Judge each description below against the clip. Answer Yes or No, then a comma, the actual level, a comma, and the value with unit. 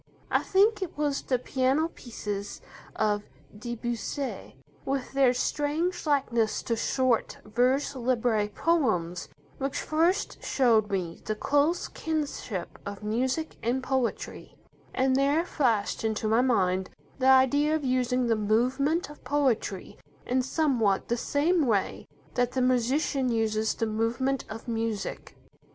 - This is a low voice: No, very high, 250 Hz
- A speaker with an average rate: No, slow, 130 wpm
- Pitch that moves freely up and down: No, average, 4.3 semitones